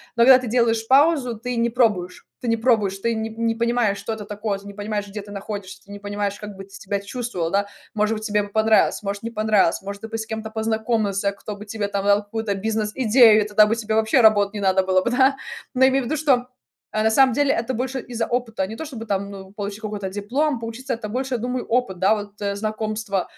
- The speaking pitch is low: No, high, 220 Hz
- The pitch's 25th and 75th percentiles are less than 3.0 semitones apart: Yes, narrow, 2.5 semitones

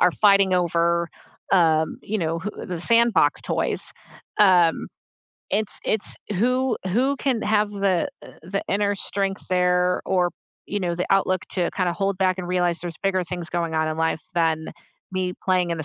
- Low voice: No, medium, 185 Hz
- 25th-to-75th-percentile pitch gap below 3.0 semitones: Yes, narrow, 2.6 semitones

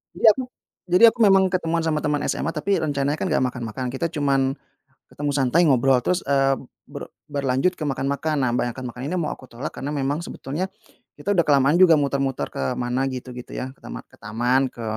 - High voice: No, medium, 140 Hz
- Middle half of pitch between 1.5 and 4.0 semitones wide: Yes, average, 3.6 semitones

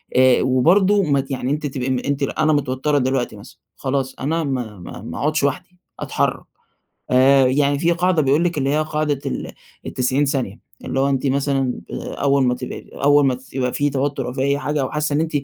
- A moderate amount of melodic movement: No, narrow, 2.3 semitones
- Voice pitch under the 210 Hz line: Yes, medium, 140 Hz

